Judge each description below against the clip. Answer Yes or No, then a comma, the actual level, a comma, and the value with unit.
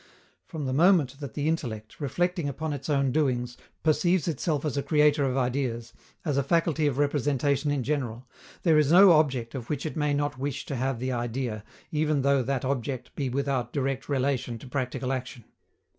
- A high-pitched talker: No, medium, 140 Hz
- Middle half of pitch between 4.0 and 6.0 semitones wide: No, average, 2.8 semitones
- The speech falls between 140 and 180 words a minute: No, average, 190 wpm